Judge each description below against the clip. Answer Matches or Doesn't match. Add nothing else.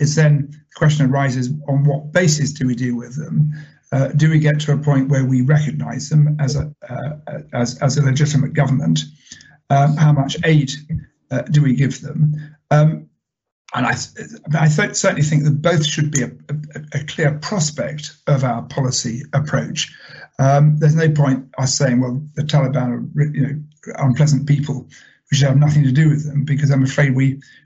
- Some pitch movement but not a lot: Doesn't match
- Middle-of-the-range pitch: Matches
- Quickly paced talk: Doesn't match